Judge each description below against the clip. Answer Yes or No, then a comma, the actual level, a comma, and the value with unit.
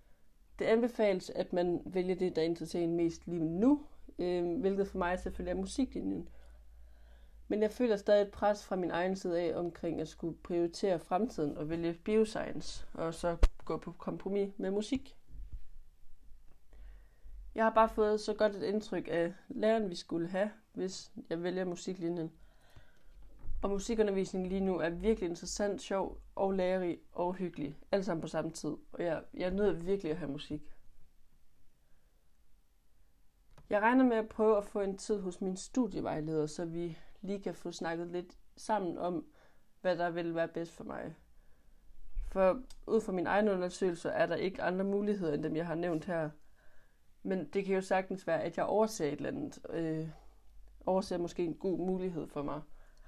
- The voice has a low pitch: No, medium, 180 Hz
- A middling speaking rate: Yes, average, 175 wpm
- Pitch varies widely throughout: No, average, 3.6 semitones